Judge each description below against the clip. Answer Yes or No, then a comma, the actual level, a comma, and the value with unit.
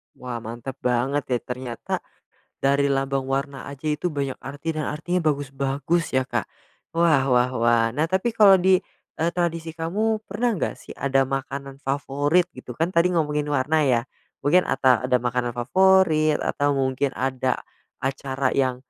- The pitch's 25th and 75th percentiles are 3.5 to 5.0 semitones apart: Yes, average, 3.8 semitones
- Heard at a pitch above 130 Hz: Yes, medium, 140 Hz